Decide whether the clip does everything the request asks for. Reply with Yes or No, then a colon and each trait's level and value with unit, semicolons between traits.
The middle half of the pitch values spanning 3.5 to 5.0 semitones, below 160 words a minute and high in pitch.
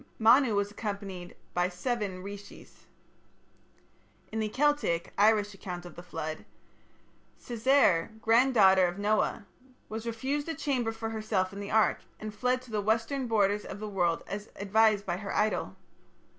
No: narrow, 2.6 semitones; average, 150 wpm; high, 210 Hz